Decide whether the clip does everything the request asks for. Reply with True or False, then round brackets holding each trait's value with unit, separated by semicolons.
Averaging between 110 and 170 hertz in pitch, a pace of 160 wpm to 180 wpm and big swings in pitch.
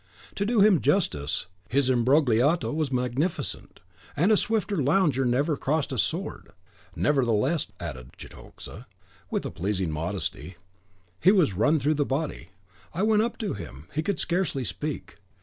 False (140 Hz; 150 wpm; 7.0 semitones)